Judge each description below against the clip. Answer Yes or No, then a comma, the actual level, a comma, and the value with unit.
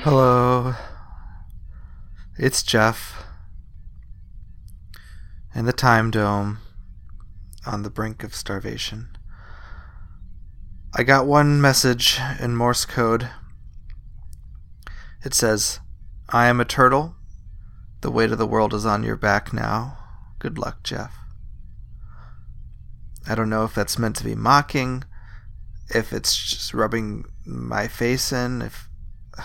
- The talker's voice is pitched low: Yes, low, 105 Hz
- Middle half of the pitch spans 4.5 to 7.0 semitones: Yes, average, 4.8 semitones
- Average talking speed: No, slow, 110 wpm